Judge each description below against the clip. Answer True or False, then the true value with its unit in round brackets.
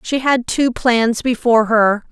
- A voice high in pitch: True (235 Hz)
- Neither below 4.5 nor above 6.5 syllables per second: False (4.1 syllables/s)